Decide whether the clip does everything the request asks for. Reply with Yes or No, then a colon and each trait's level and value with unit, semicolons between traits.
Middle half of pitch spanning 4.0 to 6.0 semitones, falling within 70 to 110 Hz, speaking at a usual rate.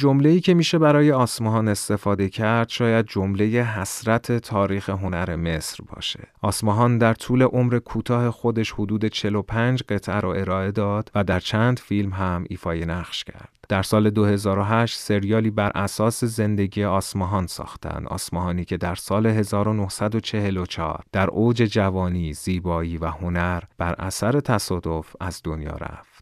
No: average, 3.3 semitones; low, 105 Hz; average, 135 wpm